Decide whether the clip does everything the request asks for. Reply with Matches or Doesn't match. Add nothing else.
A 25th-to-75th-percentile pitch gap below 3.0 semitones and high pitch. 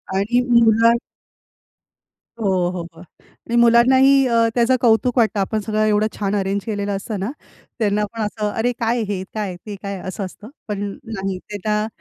Matches